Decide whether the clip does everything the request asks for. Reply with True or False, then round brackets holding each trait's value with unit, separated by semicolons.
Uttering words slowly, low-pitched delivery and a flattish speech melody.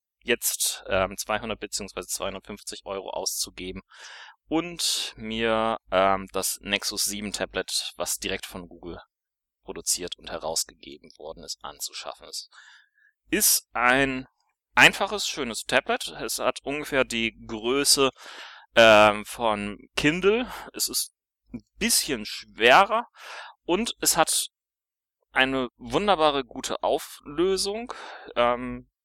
False (105 wpm; 115 Hz; 4.8 semitones)